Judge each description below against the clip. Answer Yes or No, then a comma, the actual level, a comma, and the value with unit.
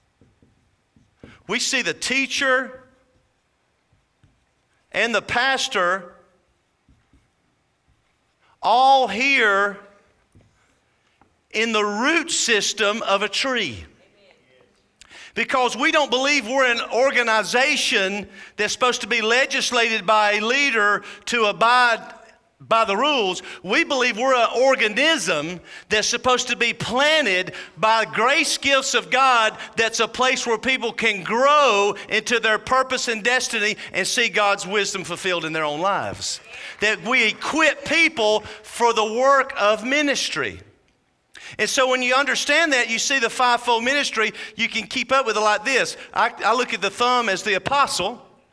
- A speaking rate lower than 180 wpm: Yes, slow, 135 wpm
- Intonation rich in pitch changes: No, average, 3.9 semitones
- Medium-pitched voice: No, high, 235 Hz